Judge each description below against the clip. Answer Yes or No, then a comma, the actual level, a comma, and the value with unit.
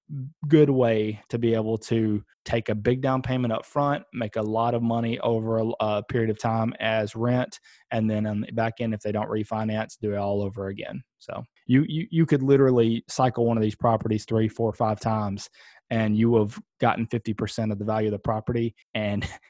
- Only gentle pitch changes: Yes, narrow, 1.8 semitones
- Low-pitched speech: Yes, low, 115 Hz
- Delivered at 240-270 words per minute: No, fast, 205 wpm